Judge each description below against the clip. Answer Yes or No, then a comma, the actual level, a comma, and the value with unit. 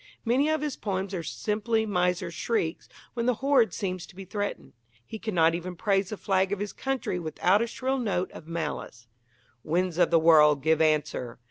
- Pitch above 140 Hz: Yes, medium, 185 Hz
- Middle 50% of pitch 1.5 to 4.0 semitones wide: No, average, 4.8 semitones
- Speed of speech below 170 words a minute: No, average, 190 wpm